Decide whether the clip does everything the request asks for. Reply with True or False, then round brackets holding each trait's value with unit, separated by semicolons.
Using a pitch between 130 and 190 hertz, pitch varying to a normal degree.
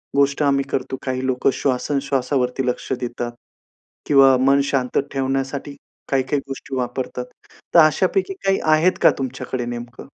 False (135 Hz; 1.7 semitones)